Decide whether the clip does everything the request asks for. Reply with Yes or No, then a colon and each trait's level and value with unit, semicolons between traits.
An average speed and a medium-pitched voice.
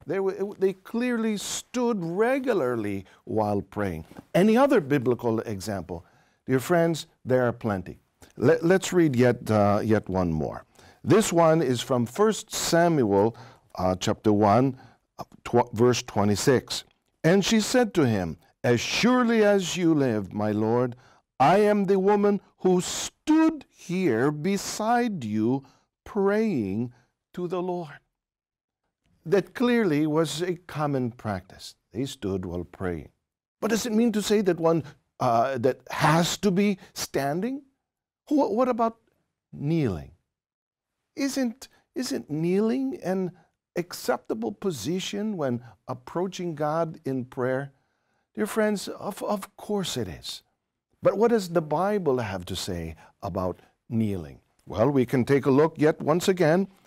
Yes: average, 135 wpm; medium, 155 Hz